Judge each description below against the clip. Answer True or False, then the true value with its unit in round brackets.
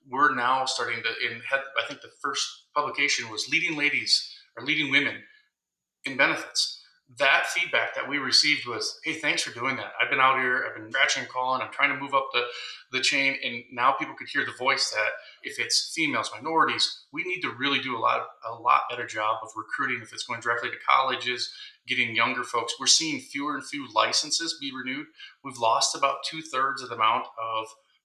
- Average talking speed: False (210 wpm)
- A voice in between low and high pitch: True (150 Hz)